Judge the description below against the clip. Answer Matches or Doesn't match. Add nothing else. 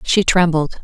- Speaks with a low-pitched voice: Doesn't match